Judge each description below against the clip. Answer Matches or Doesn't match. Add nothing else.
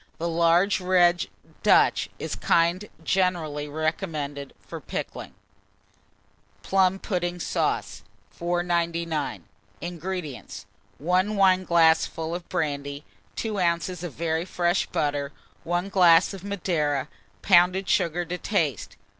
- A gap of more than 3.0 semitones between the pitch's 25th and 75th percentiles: Doesn't match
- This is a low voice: Doesn't match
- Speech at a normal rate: Doesn't match